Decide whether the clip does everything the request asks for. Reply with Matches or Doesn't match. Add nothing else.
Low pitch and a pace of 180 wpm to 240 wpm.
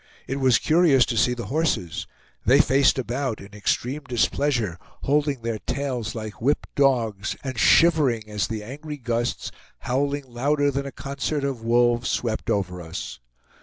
Doesn't match